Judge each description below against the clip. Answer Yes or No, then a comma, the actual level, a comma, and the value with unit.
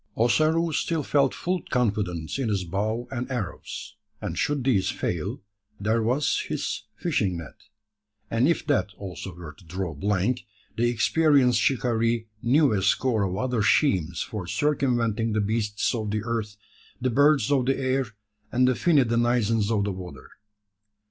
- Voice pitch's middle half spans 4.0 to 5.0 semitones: Yes, average, 4.3 semitones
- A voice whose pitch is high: No, low, 115 Hz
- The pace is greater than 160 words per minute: No, average, 155 wpm